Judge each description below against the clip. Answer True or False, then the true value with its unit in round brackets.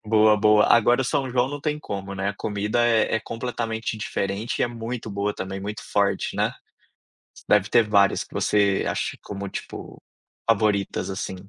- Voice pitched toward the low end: True (105 Hz)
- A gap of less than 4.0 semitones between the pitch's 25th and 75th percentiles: True (2.5 semitones)